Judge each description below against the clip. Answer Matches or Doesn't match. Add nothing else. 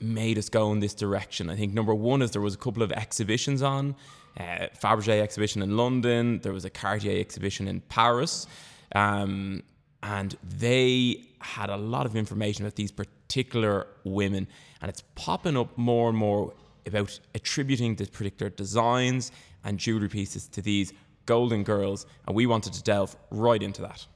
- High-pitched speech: Doesn't match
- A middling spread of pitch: Matches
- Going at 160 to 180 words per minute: Matches